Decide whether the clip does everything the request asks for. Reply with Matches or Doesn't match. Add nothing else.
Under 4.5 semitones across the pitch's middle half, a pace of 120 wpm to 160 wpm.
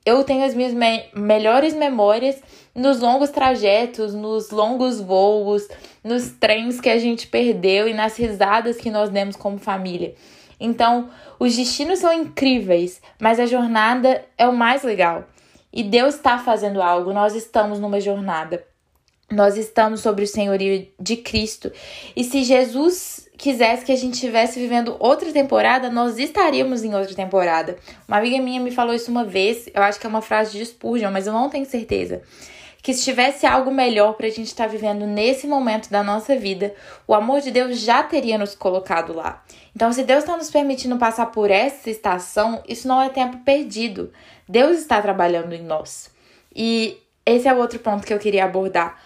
Doesn't match